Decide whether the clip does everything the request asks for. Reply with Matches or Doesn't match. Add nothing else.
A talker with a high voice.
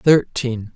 Doesn't match